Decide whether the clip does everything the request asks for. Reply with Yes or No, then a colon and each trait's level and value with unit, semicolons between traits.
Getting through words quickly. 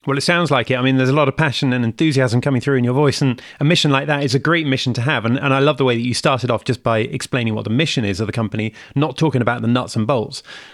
Yes: fast, 320 wpm